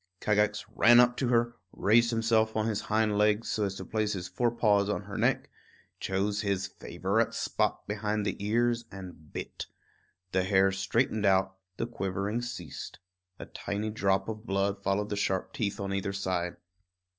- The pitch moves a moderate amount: No, narrow, 2.2 semitones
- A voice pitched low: Yes, low, 105 Hz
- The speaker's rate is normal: Yes, average, 170 wpm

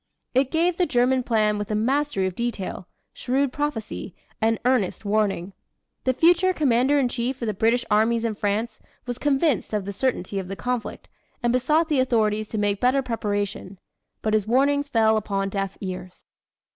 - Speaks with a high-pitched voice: Yes, high, 230 Hz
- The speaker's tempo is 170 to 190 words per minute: Yes, average, 175 wpm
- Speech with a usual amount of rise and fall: Yes, average, 4.2 semitones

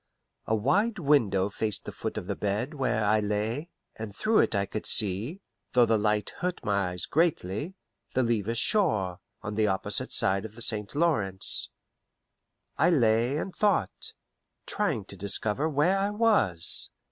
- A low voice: Yes, low, 110 Hz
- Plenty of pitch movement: Yes, wide, 7.0 semitones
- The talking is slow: No, average, 160 wpm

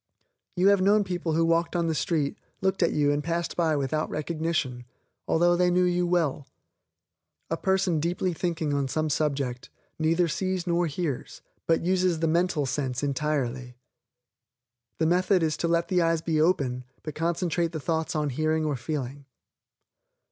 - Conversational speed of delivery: Yes, average, 165 wpm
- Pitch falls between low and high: Yes, medium, 165 Hz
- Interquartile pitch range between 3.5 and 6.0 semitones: No, average, 2.9 semitones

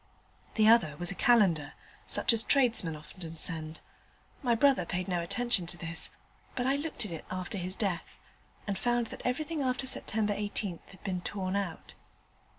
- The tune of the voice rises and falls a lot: Yes, wide, 5.7 semitones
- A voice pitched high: Yes, high, 195 Hz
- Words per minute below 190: Yes, average, 170 wpm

